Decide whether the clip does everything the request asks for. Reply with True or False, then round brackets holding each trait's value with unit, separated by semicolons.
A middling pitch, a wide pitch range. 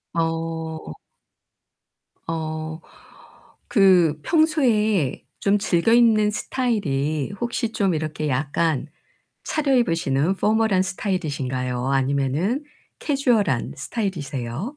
True (170 Hz; 6.8 semitones)